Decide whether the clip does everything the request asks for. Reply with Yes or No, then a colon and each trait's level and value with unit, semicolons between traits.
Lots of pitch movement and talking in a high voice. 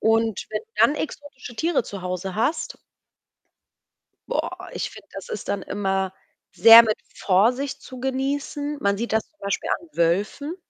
Yes: wide, 6.3 semitones; high, 225 Hz